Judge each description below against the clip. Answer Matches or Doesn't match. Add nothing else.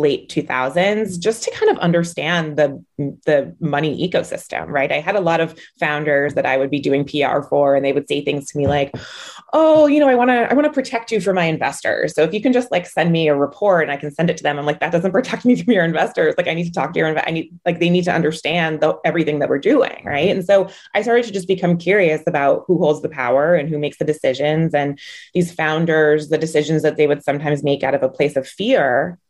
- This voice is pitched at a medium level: Matches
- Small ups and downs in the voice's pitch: Doesn't match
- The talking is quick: Matches